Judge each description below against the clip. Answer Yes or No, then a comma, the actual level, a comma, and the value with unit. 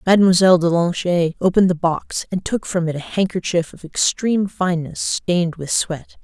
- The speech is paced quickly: No, average, 175 wpm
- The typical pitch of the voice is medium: Yes, medium, 175 Hz